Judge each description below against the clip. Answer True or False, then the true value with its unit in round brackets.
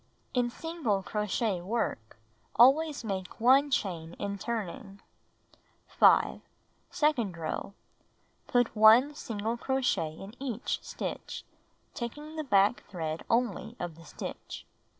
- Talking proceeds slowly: True (110 wpm)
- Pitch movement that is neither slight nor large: True (4.6 semitones)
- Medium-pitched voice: False (225 Hz)